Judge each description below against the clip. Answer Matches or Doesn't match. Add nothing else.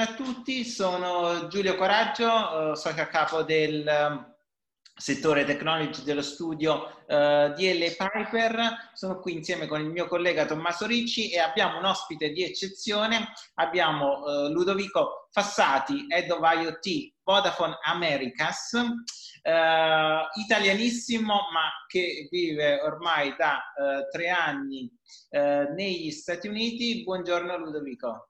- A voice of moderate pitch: Matches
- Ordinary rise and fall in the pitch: Doesn't match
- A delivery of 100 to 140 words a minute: Matches